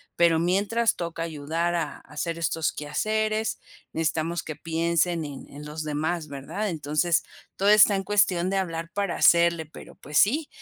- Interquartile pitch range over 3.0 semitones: Yes, average, 3.6 semitones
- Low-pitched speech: No, medium, 170 Hz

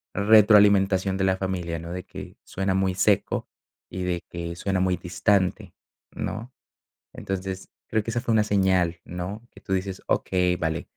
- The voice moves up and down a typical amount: No, narrow, 2.0 semitones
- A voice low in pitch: Yes, very low, 95 Hz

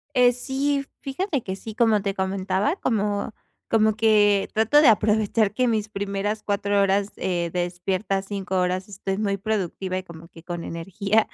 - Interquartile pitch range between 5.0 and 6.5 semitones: No, narrow, 2.5 semitones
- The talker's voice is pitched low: No, high, 205 Hz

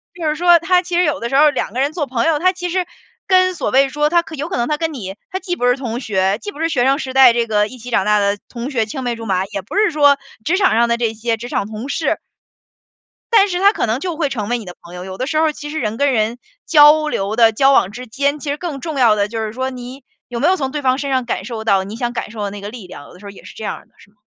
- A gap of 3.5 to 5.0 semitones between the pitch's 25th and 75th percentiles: No, wide, 5.6 semitones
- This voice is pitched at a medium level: No, very high, 255 Hz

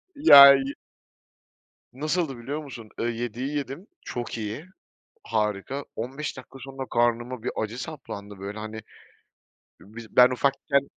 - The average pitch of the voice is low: Yes, low, 125 Hz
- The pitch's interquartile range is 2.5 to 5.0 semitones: Yes, average, 3.7 semitones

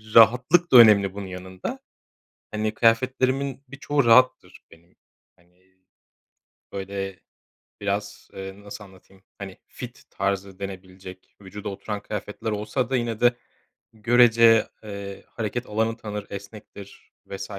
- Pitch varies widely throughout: No, average, 3.1 semitones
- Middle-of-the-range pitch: No, low, 105 Hz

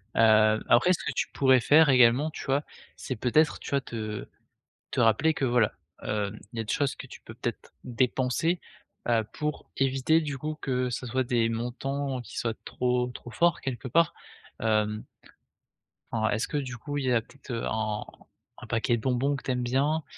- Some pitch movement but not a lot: Yes, average, 3.4 semitones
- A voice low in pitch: Yes, low, 125 Hz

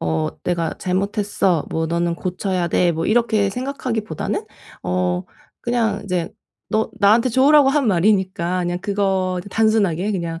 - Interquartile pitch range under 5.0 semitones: Yes, average, 4.2 semitones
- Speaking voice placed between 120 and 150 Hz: No, high, 190 Hz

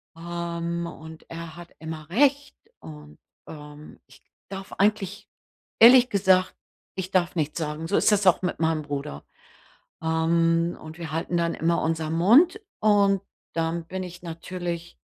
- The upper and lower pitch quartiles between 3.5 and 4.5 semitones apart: No, average, 2.7 semitones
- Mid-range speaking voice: Yes, medium, 170 Hz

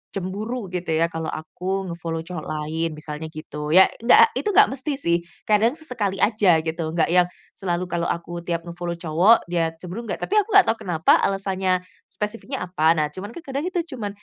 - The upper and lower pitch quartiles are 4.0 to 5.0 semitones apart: Yes, average, 4.6 semitones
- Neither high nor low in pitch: Yes, medium, 180 Hz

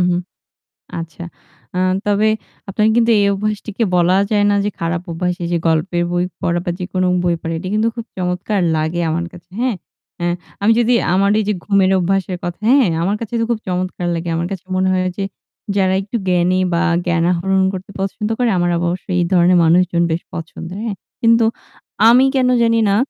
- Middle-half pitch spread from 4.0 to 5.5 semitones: No, average, 3.1 semitones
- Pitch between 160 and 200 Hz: Yes, medium, 185 Hz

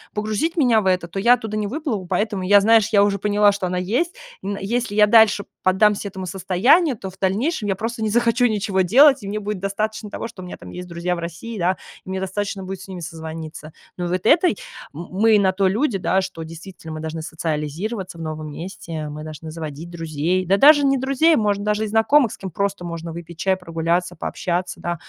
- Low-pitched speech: No, high, 195 Hz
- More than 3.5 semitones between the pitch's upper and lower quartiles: Yes, average, 3.9 semitones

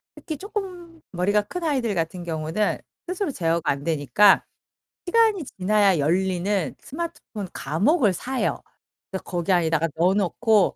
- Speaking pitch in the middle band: No, high, 200 Hz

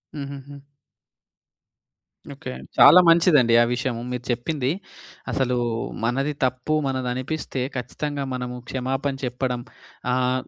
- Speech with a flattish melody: Yes, narrow, 2.2 semitones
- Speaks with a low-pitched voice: Yes, low, 130 Hz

